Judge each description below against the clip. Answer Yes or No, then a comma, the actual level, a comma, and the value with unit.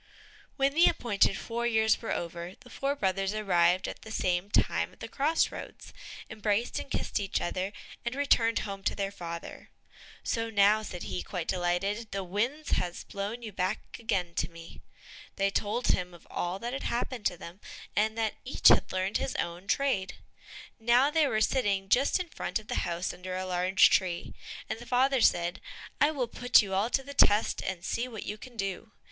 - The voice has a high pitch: Yes, high, 205 Hz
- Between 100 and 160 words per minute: No, average, 195 wpm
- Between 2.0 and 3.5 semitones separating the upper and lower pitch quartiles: No, average, 4.4 semitones